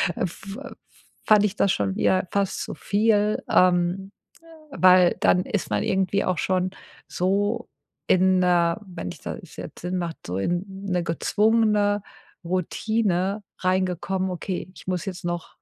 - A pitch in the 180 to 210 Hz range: Yes, medium, 185 Hz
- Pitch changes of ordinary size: No, narrow, 2.3 semitones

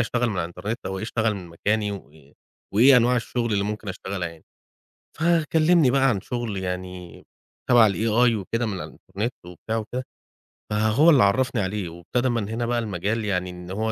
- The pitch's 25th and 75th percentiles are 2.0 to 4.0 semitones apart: No, average, 4.4 semitones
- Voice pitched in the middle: No, low, 110 Hz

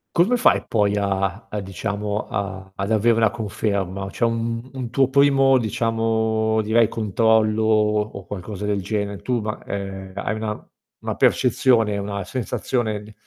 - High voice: No, low, 110 Hz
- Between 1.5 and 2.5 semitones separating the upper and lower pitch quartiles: Yes, narrow, 2.2 semitones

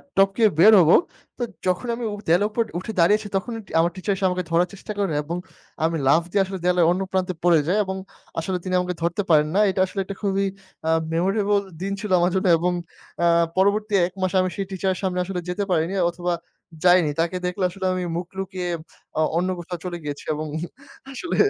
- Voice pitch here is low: No, medium, 185 Hz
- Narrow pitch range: Yes, narrow, 2.1 semitones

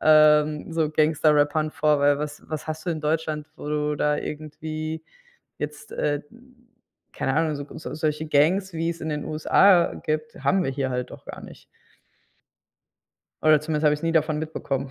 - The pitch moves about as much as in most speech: No, narrow, 1.2 semitones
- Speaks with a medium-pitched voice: Yes, medium, 155 Hz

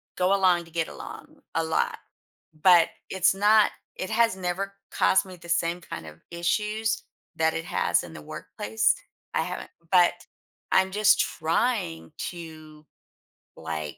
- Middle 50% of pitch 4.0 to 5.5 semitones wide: No, average, 3.2 semitones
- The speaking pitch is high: No, medium, 175 Hz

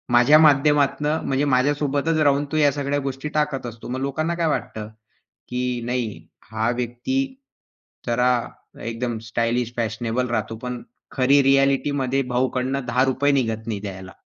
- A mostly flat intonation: No, average, 3.2 semitones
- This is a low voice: Yes, low, 130 Hz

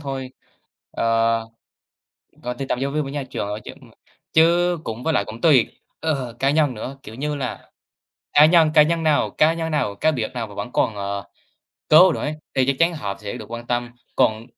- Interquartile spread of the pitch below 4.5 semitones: No, average, 5.2 semitones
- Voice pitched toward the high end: No, low, 135 Hz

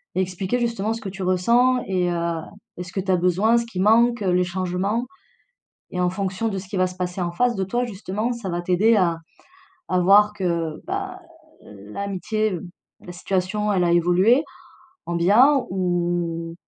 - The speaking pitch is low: No, high, 190 Hz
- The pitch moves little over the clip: No, average, 3.6 semitones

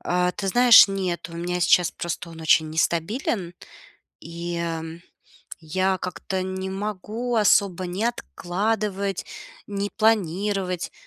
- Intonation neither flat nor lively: Yes, average, 3.0 semitones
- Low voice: No, medium, 185 Hz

